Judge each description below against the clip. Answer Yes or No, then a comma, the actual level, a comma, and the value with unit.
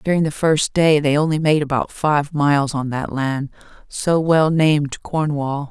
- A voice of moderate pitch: Yes, medium, 150 Hz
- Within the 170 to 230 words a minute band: Yes, average, 180 wpm